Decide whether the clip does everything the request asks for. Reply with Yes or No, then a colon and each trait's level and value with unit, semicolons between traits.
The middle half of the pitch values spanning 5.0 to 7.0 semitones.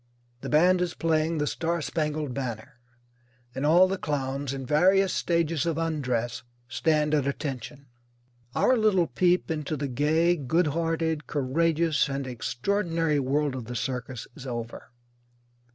No: average, 3.7 semitones